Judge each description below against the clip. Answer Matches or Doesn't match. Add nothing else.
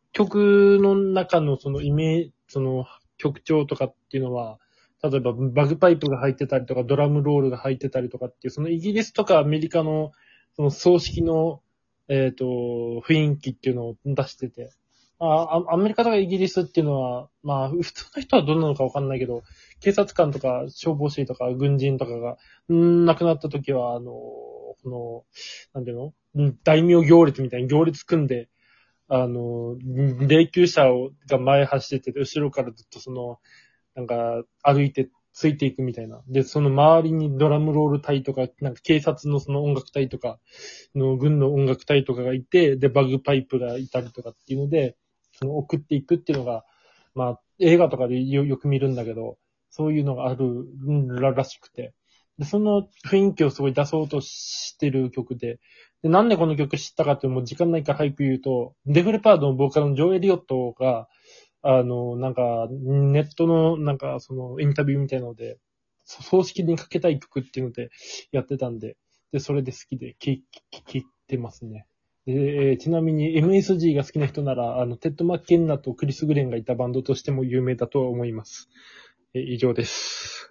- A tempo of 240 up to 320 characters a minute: Doesn't match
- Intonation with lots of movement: Doesn't match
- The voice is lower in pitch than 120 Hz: Doesn't match